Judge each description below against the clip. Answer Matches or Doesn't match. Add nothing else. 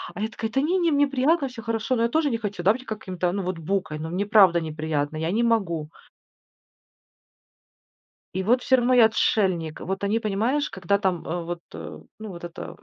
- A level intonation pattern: Doesn't match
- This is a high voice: Matches